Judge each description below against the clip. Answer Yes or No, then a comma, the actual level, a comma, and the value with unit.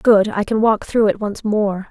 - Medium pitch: No, high, 210 Hz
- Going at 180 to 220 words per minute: No, fast, 250 wpm